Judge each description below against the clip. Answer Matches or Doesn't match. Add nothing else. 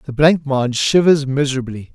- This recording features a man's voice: Matches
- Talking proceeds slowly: Matches